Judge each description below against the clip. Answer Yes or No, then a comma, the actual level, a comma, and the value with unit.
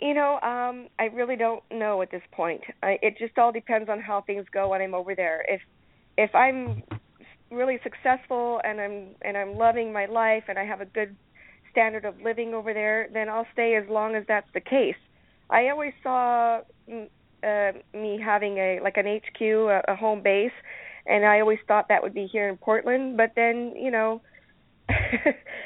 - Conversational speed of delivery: Yes, average, 190 wpm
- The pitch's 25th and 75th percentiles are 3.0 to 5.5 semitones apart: No, narrow, 2.6 semitones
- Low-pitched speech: No, high, 220 Hz